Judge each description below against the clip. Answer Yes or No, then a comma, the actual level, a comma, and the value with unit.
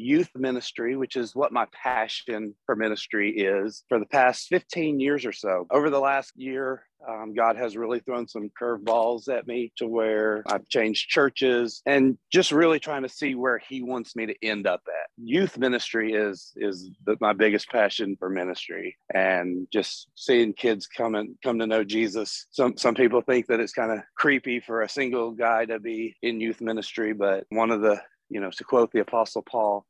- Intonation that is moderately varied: Yes, average, 3.2 semitones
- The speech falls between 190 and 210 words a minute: Yes, average, 200 wpm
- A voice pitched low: Yes, low, 115 Hz